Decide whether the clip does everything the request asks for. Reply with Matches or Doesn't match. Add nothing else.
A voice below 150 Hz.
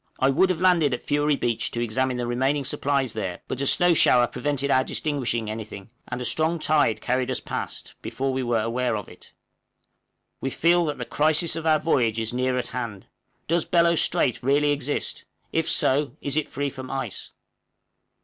Matches